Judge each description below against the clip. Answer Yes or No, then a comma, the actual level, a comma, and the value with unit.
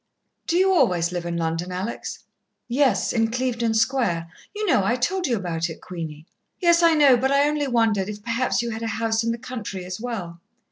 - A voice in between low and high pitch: No, high, 230 Hz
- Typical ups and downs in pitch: No, wide, 6.2 semitones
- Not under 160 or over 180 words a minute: No, fast, 205 wpm